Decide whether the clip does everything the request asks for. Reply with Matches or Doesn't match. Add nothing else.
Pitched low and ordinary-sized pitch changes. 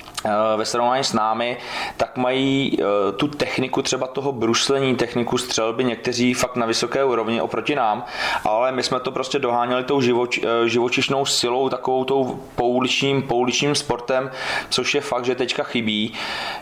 Doesn't match